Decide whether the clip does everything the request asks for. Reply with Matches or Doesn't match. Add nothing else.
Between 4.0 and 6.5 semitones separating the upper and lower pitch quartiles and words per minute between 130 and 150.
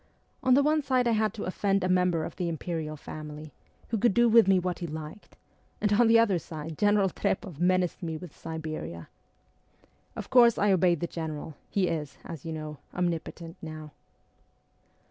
Doesn't match